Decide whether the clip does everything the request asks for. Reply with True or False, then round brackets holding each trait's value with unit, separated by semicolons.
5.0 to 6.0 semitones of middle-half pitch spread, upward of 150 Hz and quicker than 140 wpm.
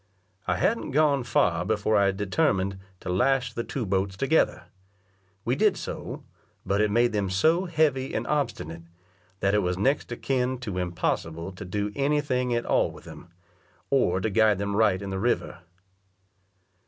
False (5.5 semitones; 105 Hz; 165 wpm)